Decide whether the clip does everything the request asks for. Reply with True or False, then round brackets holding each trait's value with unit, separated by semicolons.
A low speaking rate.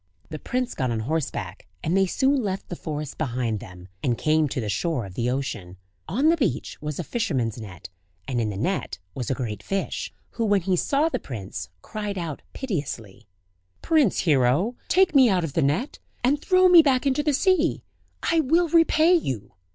False (195 wpm)